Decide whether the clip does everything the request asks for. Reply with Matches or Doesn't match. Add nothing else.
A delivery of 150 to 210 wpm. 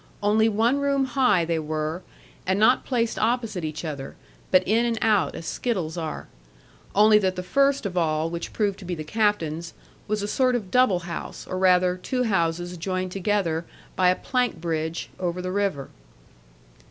Matches